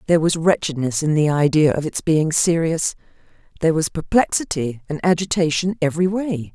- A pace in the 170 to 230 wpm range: No, average, 155 wpm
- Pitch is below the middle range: No, medium, 160 Hz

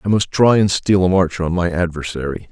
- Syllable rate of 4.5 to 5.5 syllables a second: Yes, 5.4 syllables/s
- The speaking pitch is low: Yes, very low, 90 Hz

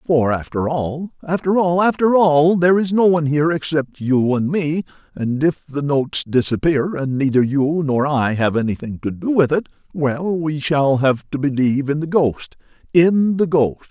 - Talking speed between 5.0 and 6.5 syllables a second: No, 4.7 syllables/s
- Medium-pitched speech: Yes, medium, 150 Hz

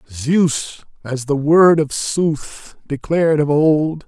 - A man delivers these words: Yes, male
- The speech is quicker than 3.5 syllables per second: No, 3.1 syllables/s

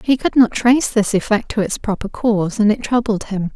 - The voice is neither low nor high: No, high, 220 Hz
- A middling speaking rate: No, fast, 235 wpm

